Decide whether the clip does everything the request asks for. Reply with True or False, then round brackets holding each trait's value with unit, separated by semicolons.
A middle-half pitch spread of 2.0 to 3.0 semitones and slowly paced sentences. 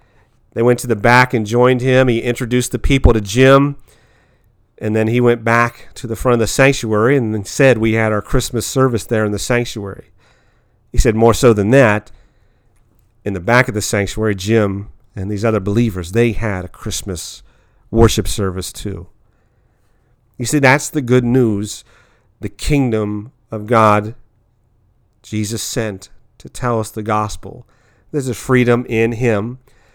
False (2.5 semitones; 165 wpm)